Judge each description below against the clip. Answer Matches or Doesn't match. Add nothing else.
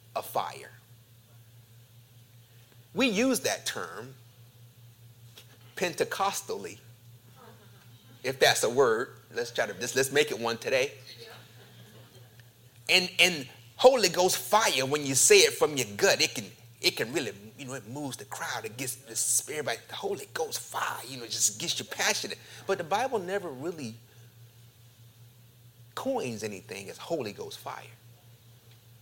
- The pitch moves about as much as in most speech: Matches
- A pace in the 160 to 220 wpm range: Doesn't match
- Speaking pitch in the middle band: Doesn't match